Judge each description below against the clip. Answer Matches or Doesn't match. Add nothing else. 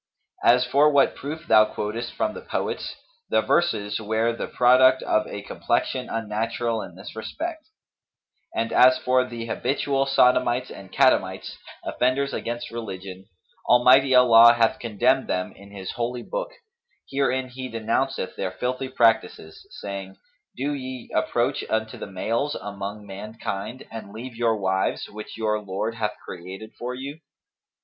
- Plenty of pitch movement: Doesn't match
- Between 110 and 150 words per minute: Matches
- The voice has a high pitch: Doesn't match